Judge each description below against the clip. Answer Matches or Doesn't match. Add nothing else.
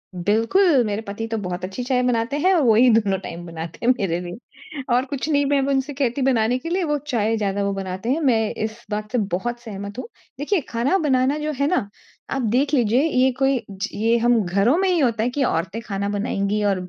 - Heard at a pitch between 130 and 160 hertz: Doesn't match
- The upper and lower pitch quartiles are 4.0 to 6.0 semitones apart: Matches